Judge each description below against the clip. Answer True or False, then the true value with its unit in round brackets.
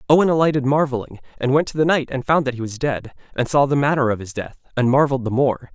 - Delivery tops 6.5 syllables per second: True (6.7 syllables/s)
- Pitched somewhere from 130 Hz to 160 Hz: True (135 Hz)